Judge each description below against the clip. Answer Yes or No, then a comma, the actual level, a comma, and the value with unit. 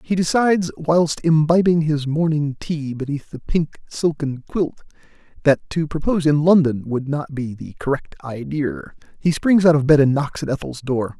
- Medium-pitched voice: Yes, medium, 150 Hz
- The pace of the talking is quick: No, average, 175 wpm